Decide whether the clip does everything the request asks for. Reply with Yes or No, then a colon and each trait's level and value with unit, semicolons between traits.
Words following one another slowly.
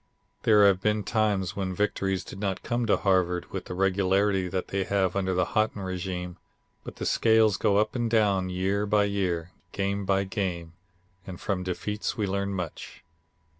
No: average, 175 wpm